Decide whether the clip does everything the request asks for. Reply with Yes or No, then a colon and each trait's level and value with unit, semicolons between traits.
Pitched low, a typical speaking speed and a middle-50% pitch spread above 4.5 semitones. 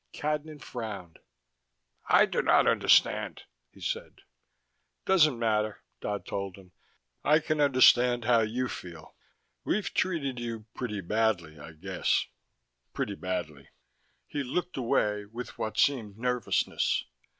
No: low, 115 Hz; slow, 120 wpm; average, 5.0 semitones